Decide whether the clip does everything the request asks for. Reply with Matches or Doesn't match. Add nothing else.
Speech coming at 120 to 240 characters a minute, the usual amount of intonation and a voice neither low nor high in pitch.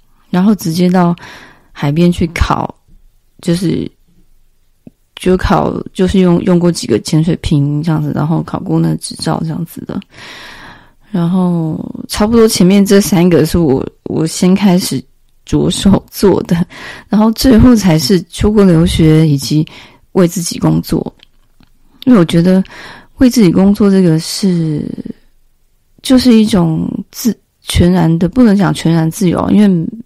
Matches